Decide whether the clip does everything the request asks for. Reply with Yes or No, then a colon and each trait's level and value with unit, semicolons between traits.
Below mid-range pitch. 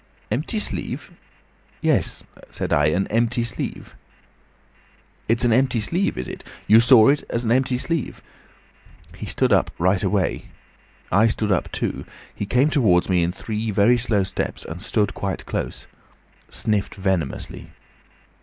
Yes: low, 110 Hz